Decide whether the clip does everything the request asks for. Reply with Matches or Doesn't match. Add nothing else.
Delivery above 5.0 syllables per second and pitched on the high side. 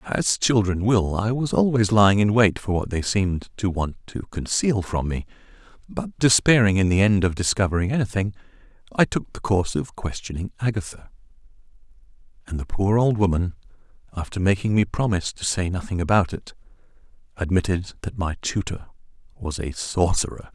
Doesn't match